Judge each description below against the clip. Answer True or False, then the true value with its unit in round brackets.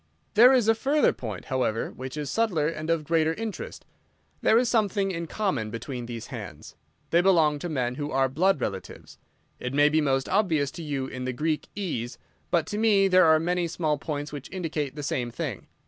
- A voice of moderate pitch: True (155 Hz)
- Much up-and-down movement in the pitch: True (5.7 semitones)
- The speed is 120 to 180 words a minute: False (200 wpm)